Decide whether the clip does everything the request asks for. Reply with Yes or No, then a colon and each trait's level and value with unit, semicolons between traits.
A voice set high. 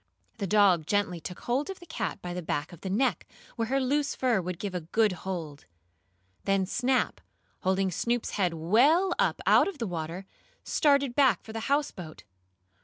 Yes: high, 205 Hz